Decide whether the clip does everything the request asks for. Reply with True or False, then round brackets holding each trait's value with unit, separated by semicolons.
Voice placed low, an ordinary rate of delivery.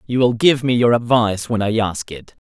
False (115 Hz; 245 wpm)